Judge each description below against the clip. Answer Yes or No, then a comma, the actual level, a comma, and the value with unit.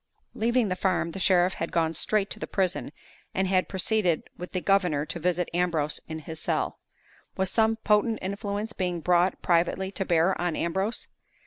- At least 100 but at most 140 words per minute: No, average, 180 wpm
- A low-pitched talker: No, medium, 185 Hz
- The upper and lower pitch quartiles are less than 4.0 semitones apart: Yes, narrow, 2.6 semitones